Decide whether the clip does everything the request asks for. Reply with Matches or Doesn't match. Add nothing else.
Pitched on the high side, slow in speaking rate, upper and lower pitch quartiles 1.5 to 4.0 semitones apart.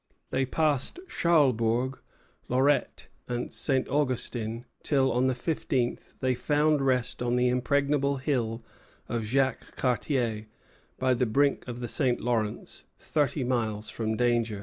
Doesn't match